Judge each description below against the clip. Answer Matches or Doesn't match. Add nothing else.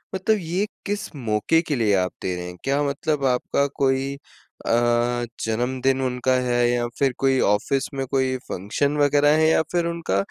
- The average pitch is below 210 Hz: Matches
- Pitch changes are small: Doesn't match